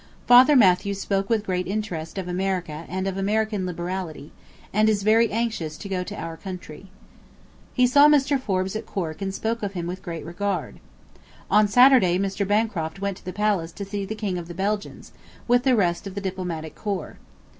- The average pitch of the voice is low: No, high, 195 Hz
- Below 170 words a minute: No, average, 190 wpm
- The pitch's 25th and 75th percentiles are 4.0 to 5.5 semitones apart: No, average, 3.0 semitones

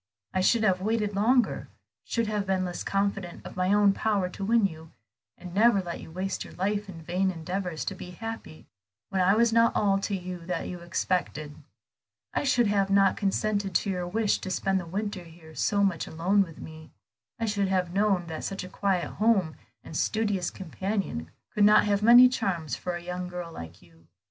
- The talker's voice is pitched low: No, high, 190 Hz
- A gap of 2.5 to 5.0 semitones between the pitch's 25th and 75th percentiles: Yes, average, 2.8 semitones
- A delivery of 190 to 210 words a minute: Yes, average, 200 wpm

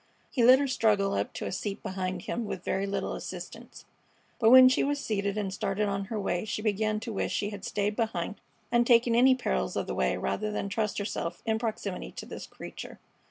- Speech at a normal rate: No, fast, 215 wpm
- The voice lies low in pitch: No, high, 210 Hz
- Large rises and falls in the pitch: No, average, 2.7 semitones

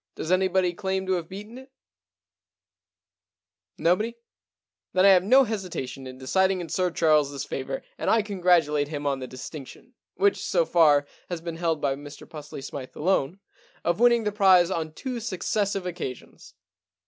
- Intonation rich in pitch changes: No, average, 4.8 semitones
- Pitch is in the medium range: Yes, medium, 180 Hz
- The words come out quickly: No, average, 170 wpm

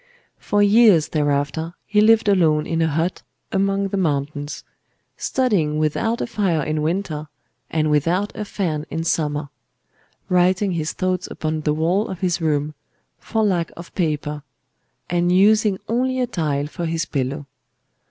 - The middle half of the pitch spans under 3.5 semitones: No, average, 4.5 semitones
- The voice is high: No, medium, 165 Hz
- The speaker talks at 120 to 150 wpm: Yes, average, 145 wpm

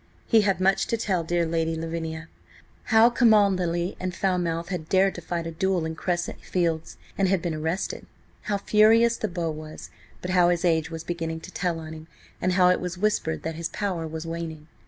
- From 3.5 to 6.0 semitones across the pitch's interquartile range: No, average, 2.7 semitones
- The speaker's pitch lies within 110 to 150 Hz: No, medium, 175 Hz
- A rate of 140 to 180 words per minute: No, average, 200 wpm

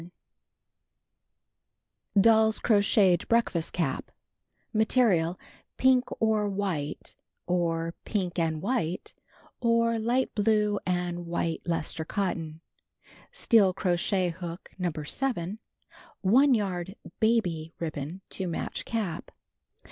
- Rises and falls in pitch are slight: No, average, 4.5 semitones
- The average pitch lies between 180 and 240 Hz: Yes, medium, 185 Hz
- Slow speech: Yes, slow, 110 wpm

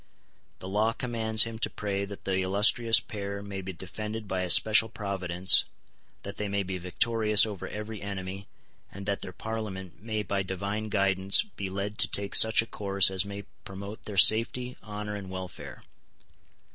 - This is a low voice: Yes, low, 100 Hz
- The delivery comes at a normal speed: Yes, average, 170 wpm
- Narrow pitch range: Yes, narrow, 2.1 semitones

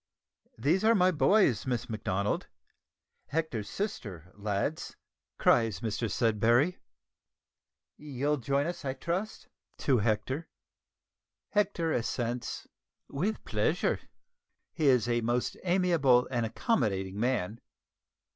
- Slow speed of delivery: Yes, slow, 100 wpm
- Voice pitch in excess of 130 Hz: No, low, 125 Hz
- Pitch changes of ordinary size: No, wide, 6.5 semitones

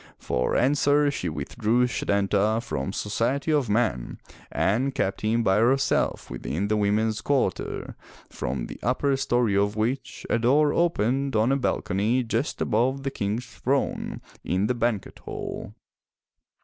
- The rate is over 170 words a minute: No, average, 140 wpm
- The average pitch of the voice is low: Yes, low, 115 Hz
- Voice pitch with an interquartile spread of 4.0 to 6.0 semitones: Yes, average, 4.5 semitones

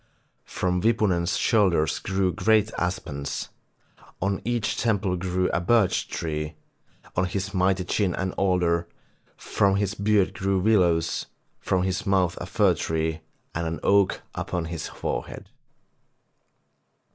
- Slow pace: Yes, slow, 125 wpm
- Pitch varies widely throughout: No, narrow, 2.6 semitones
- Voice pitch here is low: Yes, very low, 95 Hz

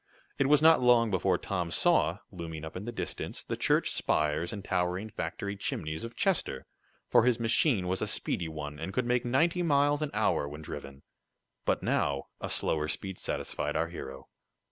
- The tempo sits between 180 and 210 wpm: Yes, average, 185 wpm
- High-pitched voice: No, very low, 95 Hz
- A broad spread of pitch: Yes, wide, 7.6 semitones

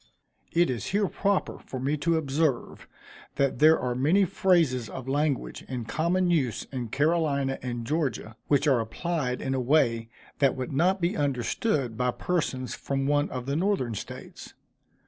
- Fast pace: No, average, 165 wpm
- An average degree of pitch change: Yes, average, 4.5 semitones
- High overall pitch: No, medium, 140 Hz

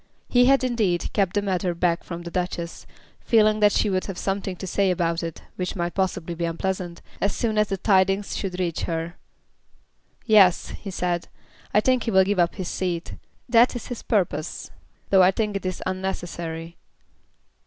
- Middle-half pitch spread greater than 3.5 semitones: No, average, 3.0 semitones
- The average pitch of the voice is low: No, medium, 185 Hz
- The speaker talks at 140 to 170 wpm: No, average, 185 wpm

